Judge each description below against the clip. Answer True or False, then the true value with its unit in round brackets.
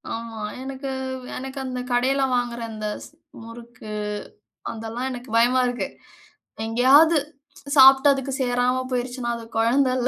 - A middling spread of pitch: False (2.0 semitones)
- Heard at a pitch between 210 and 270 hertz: True (250 Hz)